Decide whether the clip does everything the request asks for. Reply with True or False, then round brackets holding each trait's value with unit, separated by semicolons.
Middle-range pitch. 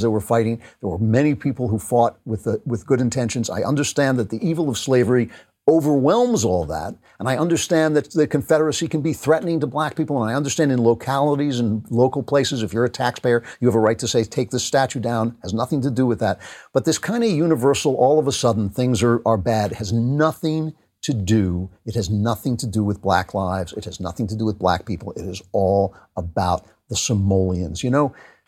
False (120 Hz)